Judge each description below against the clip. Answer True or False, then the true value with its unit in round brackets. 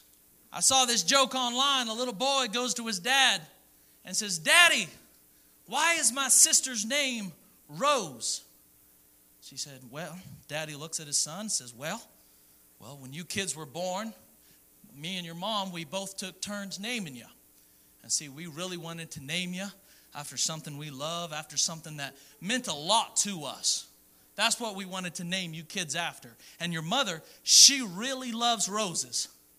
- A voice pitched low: False (175 Hz)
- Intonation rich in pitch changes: True (8.1 semitones)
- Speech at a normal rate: True (170 wpm)